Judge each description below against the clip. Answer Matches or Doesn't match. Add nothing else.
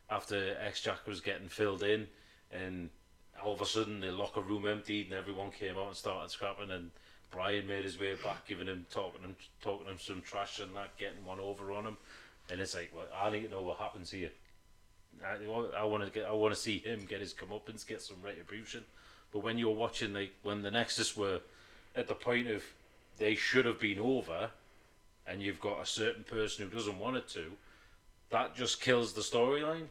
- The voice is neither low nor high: Doesn't match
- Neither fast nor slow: Doesn't match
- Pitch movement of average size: Doesn't match